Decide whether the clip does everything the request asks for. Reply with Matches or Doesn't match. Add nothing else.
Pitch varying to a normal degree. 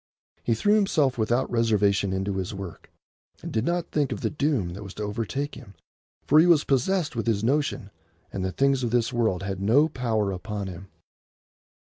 Doesn't match